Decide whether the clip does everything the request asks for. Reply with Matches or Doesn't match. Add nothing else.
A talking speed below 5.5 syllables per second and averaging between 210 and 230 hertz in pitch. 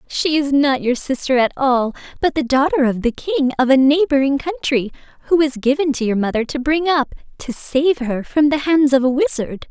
Doesn't match